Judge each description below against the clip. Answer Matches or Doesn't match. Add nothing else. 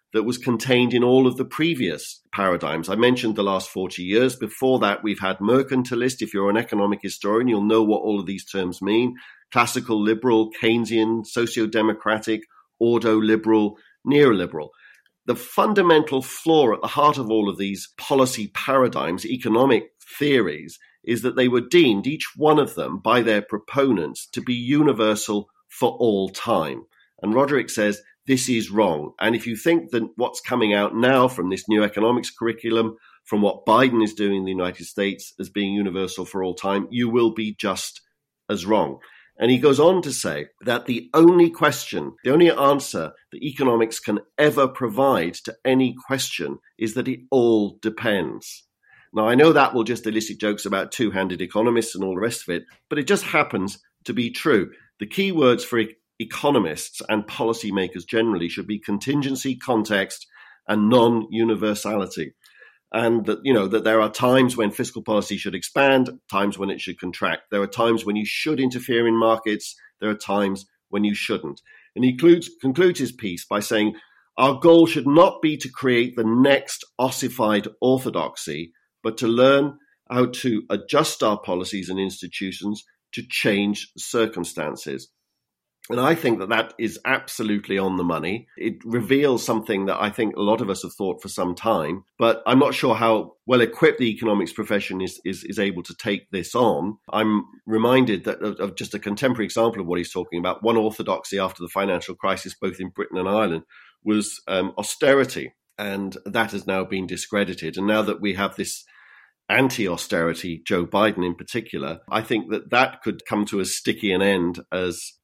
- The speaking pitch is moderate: Doesn't match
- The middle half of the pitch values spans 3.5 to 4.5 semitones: Matches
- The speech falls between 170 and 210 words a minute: Matches